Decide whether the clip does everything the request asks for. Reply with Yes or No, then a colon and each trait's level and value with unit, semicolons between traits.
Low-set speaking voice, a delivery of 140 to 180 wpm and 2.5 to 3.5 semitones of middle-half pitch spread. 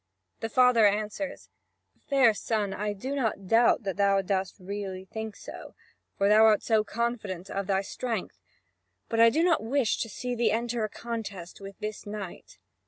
No: high, 215 Hz; average, 170 wpm; average, 3.0 semitones